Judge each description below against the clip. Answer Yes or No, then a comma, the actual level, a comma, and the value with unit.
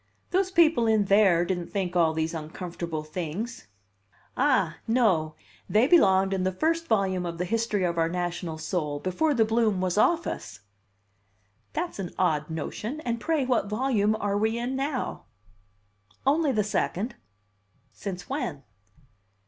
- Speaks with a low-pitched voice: No, high, 200 Hz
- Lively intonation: Yes, wide, 5.7 semitones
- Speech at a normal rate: Yes, average, 150 wpm